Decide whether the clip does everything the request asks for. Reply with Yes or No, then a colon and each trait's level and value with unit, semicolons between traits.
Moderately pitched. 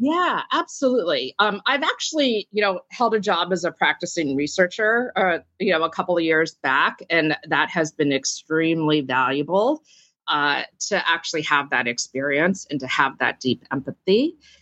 Yes: medium, 175 Hz